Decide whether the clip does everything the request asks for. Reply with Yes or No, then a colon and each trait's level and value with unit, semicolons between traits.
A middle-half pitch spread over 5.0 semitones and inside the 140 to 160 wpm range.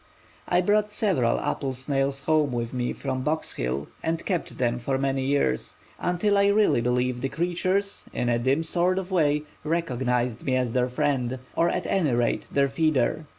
No: wide, 5.5 semitones; average, 180 wpm